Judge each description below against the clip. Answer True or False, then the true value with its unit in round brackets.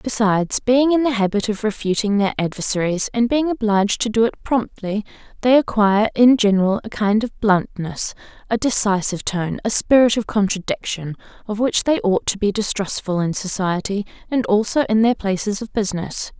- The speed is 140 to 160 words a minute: False (170 wpm)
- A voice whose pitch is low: False (210 Hz)